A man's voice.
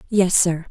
No: female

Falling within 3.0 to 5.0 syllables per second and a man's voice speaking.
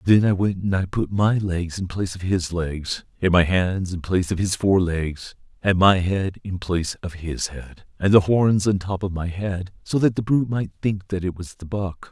Yes: 4.8 syllables/s; male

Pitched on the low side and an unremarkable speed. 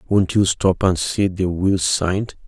Yes: very low, 90 Hz; average, 195 wpm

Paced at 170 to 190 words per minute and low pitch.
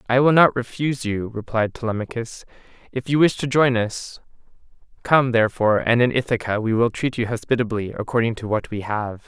Yes: average, 180 wpm; low, 120 Hz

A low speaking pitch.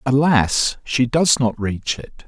Yes: low, 125 Hz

